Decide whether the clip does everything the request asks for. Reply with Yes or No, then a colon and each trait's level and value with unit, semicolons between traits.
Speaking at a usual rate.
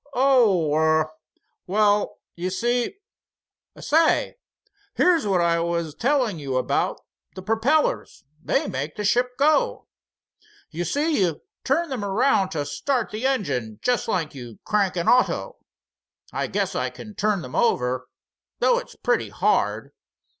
No: slow, 130 wpm